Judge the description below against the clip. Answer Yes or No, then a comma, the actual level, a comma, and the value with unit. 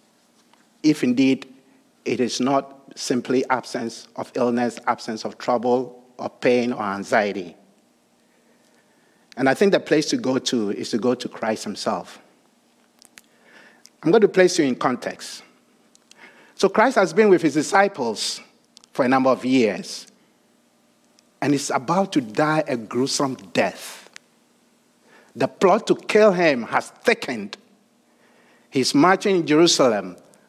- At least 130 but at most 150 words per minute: Yes, slow, 135 wpm